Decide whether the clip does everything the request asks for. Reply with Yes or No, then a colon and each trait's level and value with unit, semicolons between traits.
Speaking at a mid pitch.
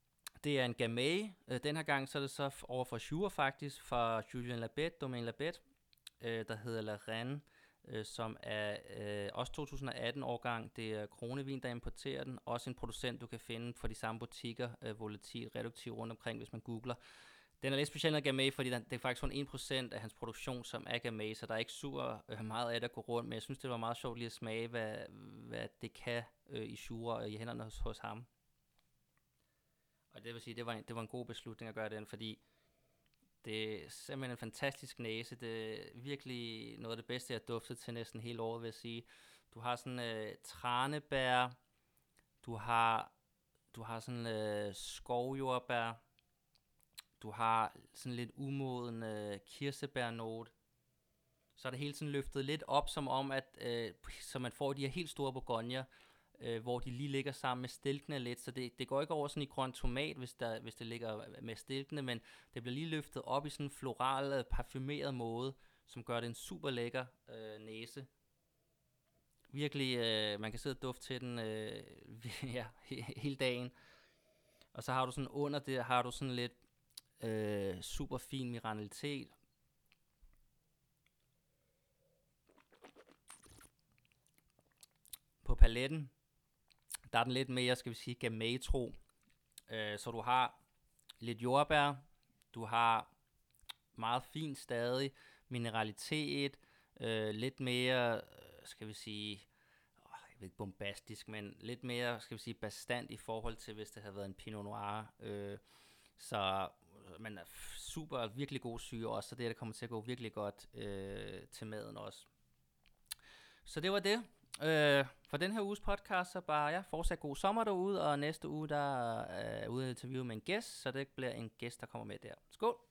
No: low, 120 Hz